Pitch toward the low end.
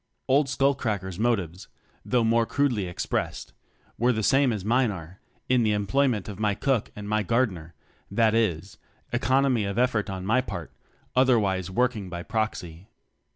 Yes: low, 110 Hz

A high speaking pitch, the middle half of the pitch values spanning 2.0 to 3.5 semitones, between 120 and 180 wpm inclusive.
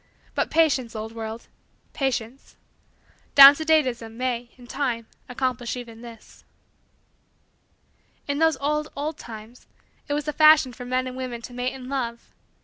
Yes: very high, 255 Hz; average, 3.2 semitones; average, 155 wpm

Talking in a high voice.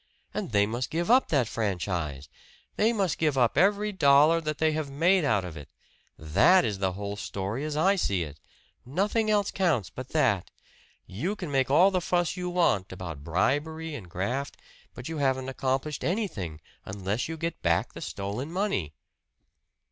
No: low, 135 Hz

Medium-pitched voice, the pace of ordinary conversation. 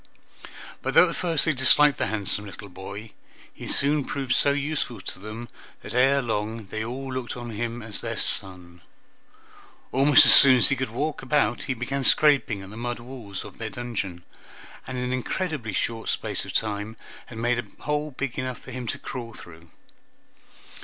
No: low, 120 Hz; average, 185 wpm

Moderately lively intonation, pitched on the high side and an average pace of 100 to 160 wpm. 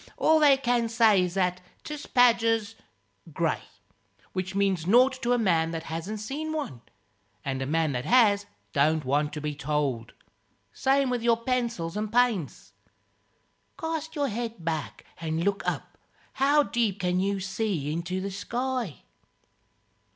No: wide, 7.0 semitones; high, 200 Hz; average, 150 wpm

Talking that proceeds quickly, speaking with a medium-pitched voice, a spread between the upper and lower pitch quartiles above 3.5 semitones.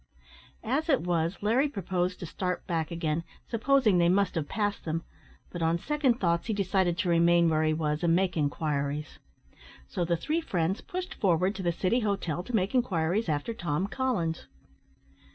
No: average, 175 wpm; medium, 180 Hz; average, 4.4 semitones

